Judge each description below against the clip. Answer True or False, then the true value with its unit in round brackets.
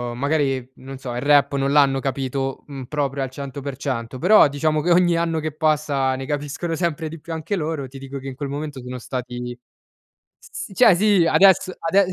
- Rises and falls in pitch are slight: False (3.2 semitones)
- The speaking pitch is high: False (140 Hz)